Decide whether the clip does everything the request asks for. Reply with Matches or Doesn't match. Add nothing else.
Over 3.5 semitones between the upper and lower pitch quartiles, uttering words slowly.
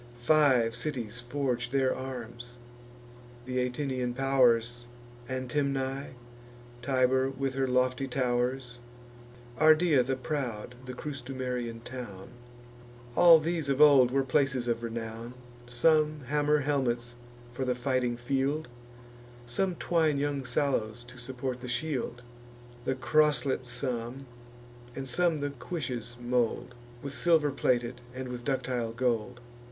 Doesn't match